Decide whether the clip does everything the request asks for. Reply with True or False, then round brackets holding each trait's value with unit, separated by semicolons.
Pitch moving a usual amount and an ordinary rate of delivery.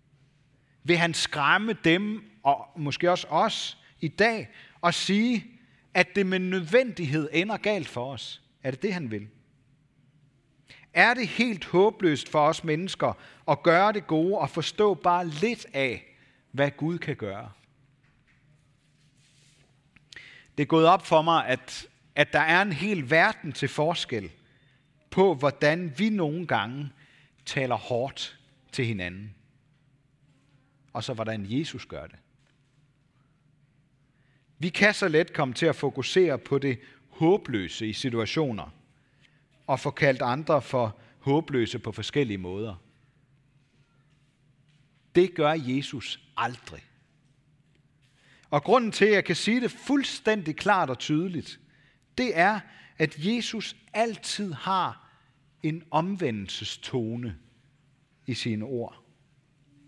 False (3.8 semitones; 125 wpm)